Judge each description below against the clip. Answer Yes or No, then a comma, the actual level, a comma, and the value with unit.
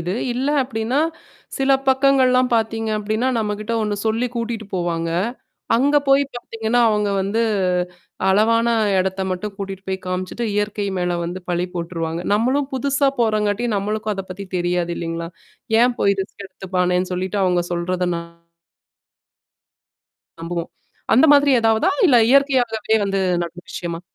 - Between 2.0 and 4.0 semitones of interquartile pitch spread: No, average, 4.5 semitones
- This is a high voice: Yes, high, 210 Hz